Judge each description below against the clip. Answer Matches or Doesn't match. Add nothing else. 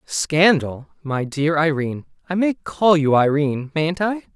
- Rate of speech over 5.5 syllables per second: Doesn't match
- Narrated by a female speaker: Doesn't match